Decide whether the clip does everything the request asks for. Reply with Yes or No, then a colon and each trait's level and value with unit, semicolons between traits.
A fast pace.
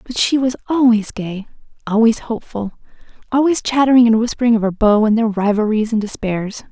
No: average, 170 wpm